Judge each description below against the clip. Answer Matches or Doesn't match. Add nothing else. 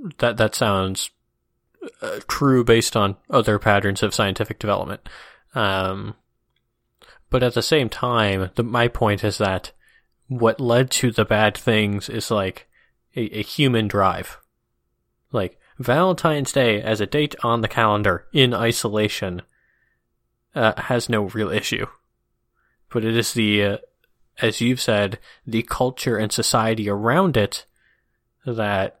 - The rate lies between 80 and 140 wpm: Matches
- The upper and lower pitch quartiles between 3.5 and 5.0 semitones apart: Doesn't match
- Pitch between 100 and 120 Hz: Matches